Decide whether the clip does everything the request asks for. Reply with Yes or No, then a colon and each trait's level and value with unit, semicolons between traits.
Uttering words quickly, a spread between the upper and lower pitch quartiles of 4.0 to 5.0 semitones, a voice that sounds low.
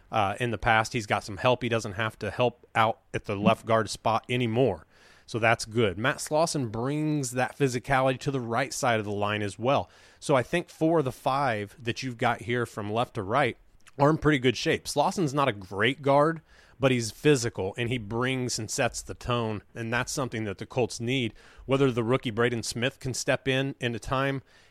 No: fast, 220 wpm; average, 3.3 semitones; low, 120 Hz